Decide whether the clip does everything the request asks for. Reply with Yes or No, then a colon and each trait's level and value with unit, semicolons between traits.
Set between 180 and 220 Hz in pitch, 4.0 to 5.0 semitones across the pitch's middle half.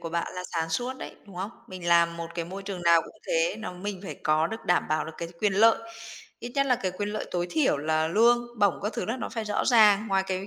Yes: high, 195 Hz; average, 4.6 semitones